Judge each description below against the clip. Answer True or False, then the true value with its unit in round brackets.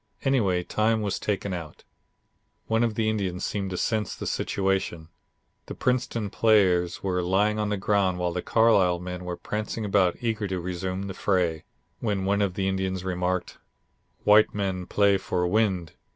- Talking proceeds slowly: False (165 wpm)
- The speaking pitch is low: True (95 Hz)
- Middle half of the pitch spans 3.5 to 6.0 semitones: False (2.7 semitones)